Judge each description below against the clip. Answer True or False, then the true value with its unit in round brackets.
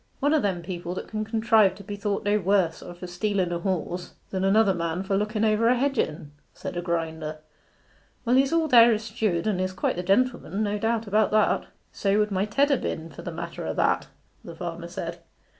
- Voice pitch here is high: True (200 Hz)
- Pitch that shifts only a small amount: False (3.6 semitones)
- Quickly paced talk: True (225 wpm)